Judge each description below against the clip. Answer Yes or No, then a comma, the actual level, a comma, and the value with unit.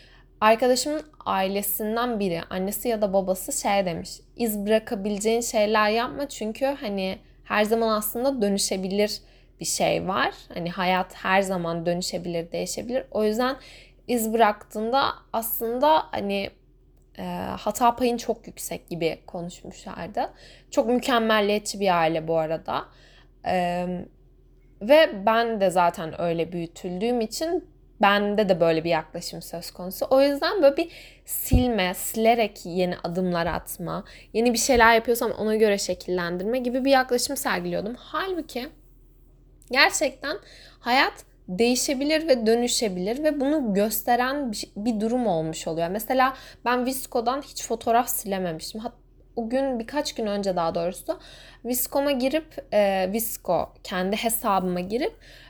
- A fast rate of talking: No, average, 125 wpm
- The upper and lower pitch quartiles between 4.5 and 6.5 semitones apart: Yes, average, 5.1 semitones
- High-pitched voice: Yes, high, 220 Hz